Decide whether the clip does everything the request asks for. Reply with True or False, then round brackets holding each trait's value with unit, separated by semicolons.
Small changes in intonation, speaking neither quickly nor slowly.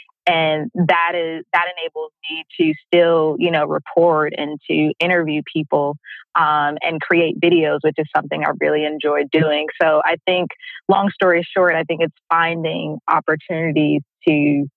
True (2.3 semitones; 155 wpm)